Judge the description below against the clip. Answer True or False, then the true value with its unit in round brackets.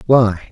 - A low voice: True (110 Hz)